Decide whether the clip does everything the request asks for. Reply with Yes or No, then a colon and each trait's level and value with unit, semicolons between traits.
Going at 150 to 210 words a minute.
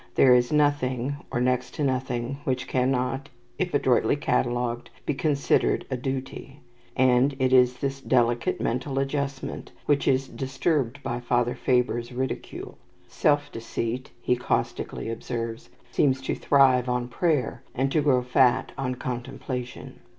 No: slow, 135 wpm